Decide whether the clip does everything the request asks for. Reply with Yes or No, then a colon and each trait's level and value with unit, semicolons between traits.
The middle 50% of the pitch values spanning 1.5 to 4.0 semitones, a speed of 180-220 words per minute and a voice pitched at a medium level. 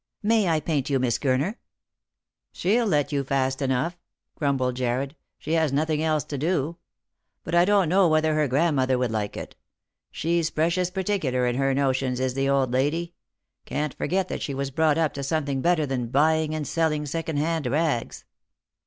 Yes: average, 3.7 semitones; average, 190 wpm; medium, 150 Hz